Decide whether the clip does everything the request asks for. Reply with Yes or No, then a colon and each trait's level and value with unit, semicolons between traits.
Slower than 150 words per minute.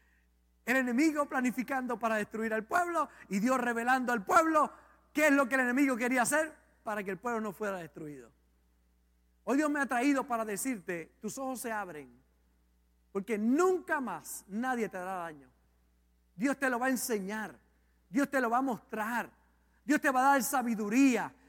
No: average, 175 wpm